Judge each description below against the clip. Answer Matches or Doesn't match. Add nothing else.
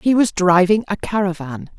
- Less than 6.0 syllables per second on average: Matches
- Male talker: Doesn't match